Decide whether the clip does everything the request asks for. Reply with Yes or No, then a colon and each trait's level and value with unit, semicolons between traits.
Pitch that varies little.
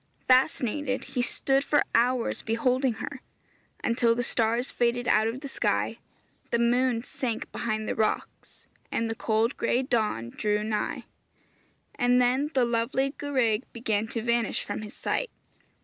Yes: narrow, 2.3 semitones